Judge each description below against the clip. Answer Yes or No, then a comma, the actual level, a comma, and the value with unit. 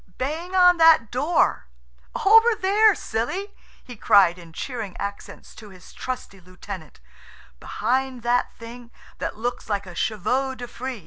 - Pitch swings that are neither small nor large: No, wide, 6.9 semitones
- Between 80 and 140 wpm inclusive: Yes, slow, 135 wpm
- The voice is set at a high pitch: Yes, high, 240 Hz